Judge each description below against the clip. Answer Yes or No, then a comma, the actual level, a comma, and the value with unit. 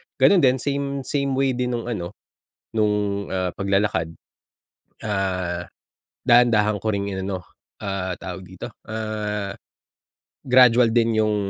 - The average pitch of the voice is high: No, low, 105 Hz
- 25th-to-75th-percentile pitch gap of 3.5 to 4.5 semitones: Yes, average, 3.9 semitones